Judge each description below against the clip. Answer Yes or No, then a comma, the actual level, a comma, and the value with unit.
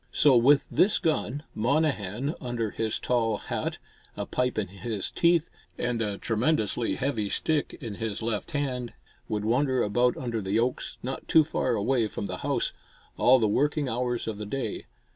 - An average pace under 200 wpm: Yes, average, 170 wpm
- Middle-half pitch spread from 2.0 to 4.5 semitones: Yes, average, 4.0 semitones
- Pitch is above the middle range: No, low, 120 Hz